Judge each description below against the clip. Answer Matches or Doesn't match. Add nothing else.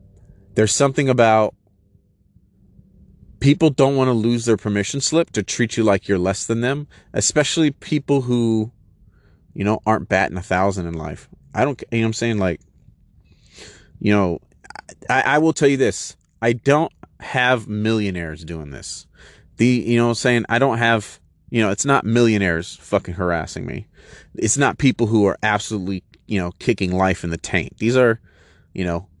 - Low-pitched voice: Matches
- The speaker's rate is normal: Matches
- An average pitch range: Matches